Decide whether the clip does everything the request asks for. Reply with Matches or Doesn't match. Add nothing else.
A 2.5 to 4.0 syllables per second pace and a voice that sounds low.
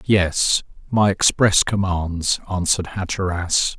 Matches